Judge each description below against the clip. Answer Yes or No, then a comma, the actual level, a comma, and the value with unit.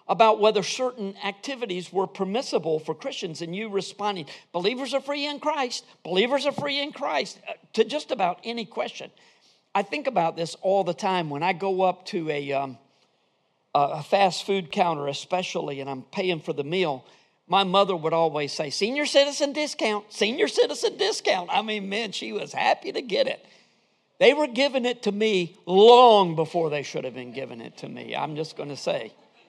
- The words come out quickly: No, average, 185 wpm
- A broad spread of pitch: Yes, wide, 6.5 semitones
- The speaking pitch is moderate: No, high, 195 Hz